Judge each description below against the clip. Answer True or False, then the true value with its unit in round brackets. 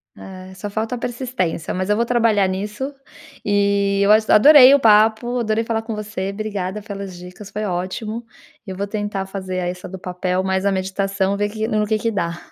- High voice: True (205 Hz)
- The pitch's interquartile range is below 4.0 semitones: True (2.6 semitones)